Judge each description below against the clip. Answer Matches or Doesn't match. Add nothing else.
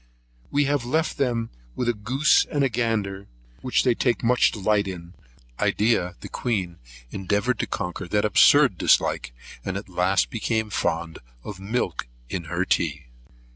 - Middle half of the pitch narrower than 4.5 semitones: Doesn't match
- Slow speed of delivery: Doesn't match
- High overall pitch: Doesn't match